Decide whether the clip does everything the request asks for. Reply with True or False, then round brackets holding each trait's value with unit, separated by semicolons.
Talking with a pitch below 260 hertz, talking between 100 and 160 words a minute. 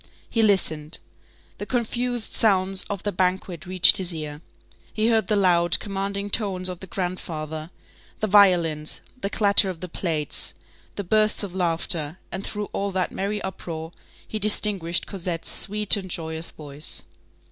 True (185 Hz; 150 wpm)